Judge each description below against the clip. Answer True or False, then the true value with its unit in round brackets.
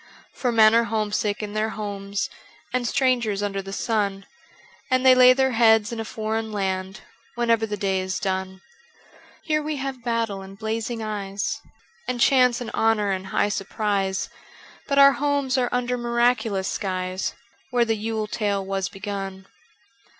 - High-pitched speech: True (220 Hz)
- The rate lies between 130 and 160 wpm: True (155 wpm)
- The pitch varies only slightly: False (3.5 semitones)